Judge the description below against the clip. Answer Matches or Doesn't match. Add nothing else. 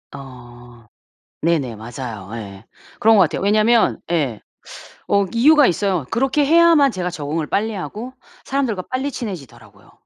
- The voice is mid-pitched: Matches